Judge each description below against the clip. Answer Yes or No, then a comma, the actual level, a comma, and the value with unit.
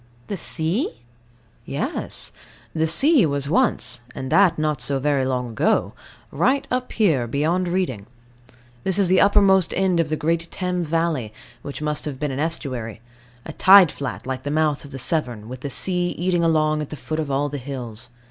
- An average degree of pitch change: Yes, average, 4.8 semitones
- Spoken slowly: No, average, 185 wpm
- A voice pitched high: No, medium, 155 Hz